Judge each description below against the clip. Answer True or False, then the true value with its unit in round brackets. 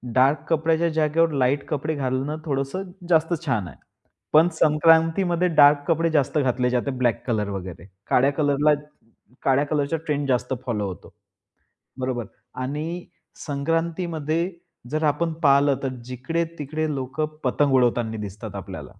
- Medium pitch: True (145 Hz)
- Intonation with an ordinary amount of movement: True (3.9 semitones)